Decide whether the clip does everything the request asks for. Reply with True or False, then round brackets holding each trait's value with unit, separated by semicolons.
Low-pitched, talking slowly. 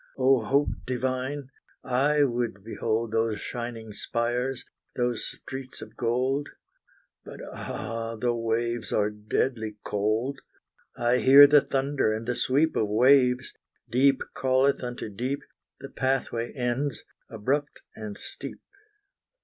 True (125 Hz; 125 wpm)